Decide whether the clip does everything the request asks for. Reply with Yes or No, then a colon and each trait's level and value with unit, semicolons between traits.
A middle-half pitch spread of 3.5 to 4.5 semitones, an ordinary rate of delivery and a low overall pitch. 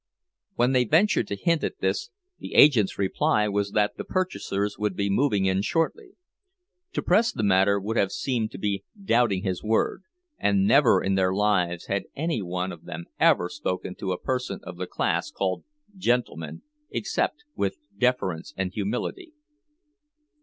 No: average, 5.0 semitones; average, 165 wpm; low, 105 Hz